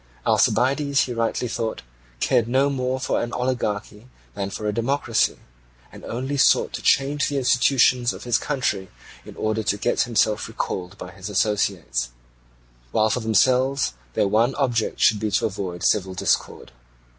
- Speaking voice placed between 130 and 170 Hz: No, low, 115 Hz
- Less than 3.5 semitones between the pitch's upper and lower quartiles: No, average, 3.8 semitones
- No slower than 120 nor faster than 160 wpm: Yes, average, 155 wpm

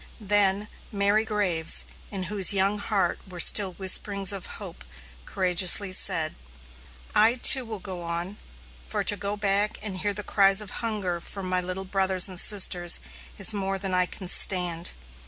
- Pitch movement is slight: Yes, narrow, 2.1 semitones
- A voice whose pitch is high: Yes, high, 195 Hz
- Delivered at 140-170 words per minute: Yes, average, 160 wpm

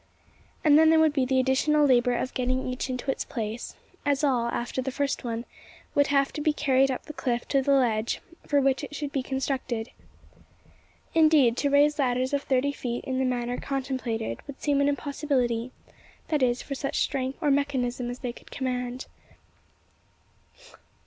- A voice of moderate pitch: No, very high, 265 Hz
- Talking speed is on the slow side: No, average, 180 wpm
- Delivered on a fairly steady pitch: Yes, narrow, 2.3 semitones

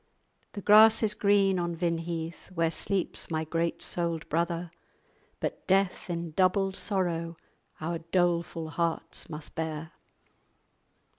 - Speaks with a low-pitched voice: No, medium, 170 Hz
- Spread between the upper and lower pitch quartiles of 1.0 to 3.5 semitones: Yes, narrow, 2.4 semitones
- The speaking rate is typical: No, slow, 120 wpm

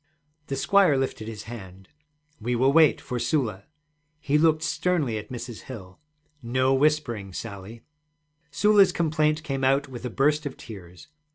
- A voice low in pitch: Yes, low, 130 Hz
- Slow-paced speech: No, average, 150 wpm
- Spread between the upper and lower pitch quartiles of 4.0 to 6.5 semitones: Yes, average, 5.2 semitones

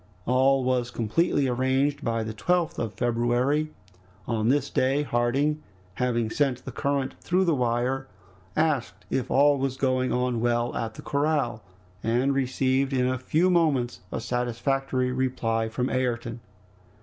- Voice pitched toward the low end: Yes, low, 130 Hz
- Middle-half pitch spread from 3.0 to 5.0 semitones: No, narrow, 2.5 semitones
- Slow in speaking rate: No, average, 145 wpm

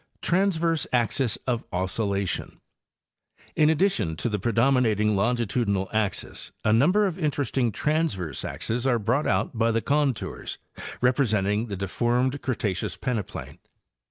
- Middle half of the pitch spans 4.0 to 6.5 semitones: Yes, average, 5.1 semitones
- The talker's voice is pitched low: Yes, low, 120 Hz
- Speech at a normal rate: No, slow, 130 wpm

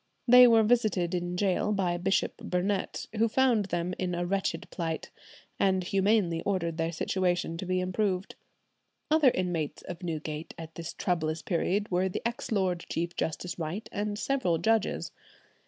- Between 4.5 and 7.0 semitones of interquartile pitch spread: No, average, 3.1 semitones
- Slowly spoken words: No, average, 155 wpm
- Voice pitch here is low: No, medium, 185 Hz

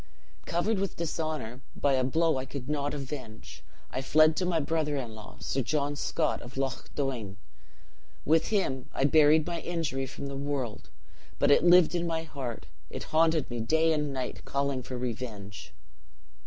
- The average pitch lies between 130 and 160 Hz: Yes, medium, 140 Hz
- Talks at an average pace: Yes, average, 170 wpm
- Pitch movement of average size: Yes, average, 3.6 semitones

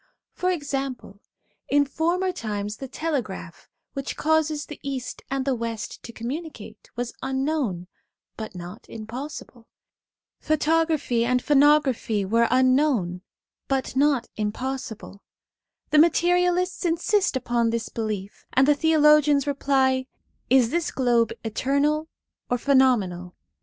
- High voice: Yes, very high, 265 Hz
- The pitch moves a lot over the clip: No, average, 4.7 semitones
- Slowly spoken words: Yes, slow, 115 wpm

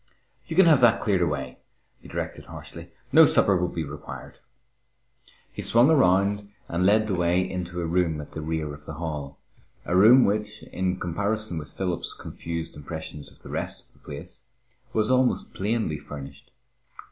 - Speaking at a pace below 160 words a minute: No, average, 170 wpm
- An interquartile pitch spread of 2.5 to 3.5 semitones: No, average, 5.0 semitones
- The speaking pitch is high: No, very low, 90 Hz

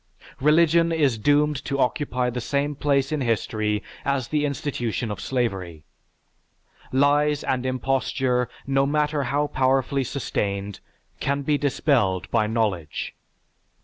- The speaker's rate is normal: No, slow, 120 wpm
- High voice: No, low, 135 Hz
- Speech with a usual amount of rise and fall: Yes, average, 3.9 semitones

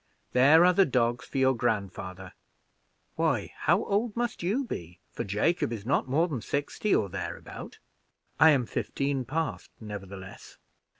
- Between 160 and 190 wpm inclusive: No, average, 145 wpm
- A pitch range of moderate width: No, wide, 8.3 semitones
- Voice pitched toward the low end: Yes, low, 130 Hz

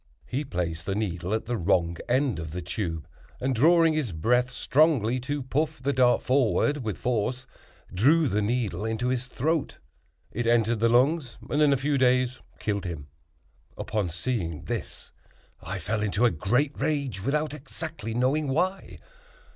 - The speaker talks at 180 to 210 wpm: No, average, 165 wpm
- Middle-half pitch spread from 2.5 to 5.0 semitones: No, wide, 5.5 semitones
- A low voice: Yes, low, 125 Hz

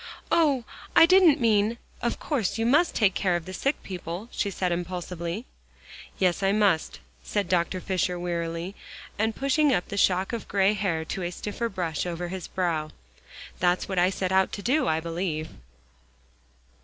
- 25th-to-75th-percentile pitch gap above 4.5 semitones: No, average, 3.9 semitones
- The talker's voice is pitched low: No, high, 190 Hz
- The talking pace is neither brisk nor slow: Yes, average, 170 wpm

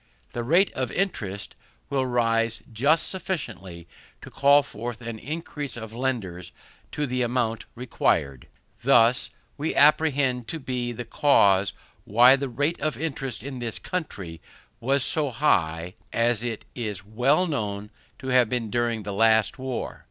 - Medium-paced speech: Yes, average, 145 wpm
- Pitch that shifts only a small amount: No, average, 4.1 semitones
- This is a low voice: Yes, low, 120 Hz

